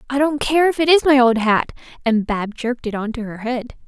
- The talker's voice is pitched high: Yes, very high, 250 Hz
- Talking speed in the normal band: No, fast, 265 wpm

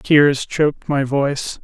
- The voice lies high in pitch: No, medium, 140 Hz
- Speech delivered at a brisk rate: No, average, 145 wpm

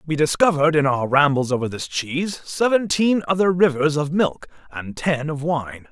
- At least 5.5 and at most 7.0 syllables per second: No, 5.0 syllables/s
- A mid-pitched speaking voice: Yes, medium, 155 Hz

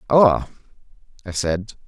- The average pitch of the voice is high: No, low, 105 Hz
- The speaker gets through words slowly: Yes, slow, 95 wpm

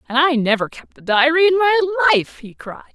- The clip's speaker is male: No, female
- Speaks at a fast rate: Yes, fast, 225 wpm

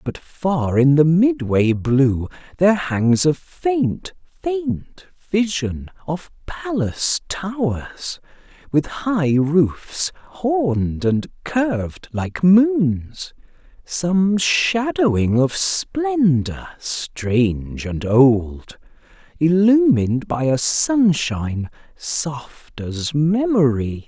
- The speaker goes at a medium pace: No, slow, 90 wpm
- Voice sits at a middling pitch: Yes, medium, 160 Hz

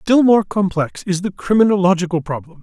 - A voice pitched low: No, high, 190 Hz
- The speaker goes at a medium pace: Yes, average, 160 wpm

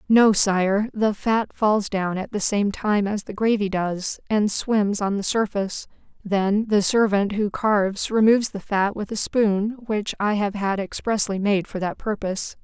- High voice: Yes, high, 205 Hz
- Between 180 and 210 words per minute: Yes, average, 185 wpm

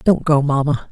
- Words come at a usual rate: Yes, average, 195 wpm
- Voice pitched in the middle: Yes, medium, 145 Hz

